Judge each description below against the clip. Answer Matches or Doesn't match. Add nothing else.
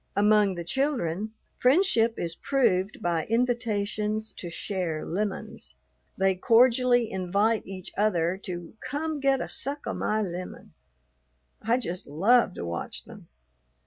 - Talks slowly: Matches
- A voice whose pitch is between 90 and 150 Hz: Doesn't match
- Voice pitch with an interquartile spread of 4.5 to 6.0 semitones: Matches